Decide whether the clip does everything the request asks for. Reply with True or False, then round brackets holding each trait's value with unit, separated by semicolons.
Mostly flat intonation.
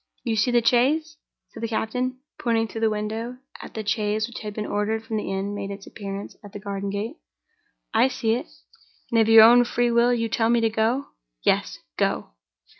True (2.3 semitones)